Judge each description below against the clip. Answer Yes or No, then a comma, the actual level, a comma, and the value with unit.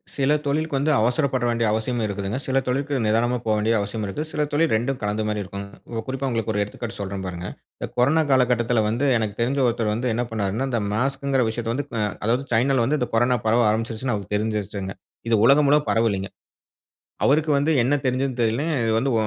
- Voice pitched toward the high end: No, low, 120 Hz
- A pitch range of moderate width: Yes, average, 3.8 semitones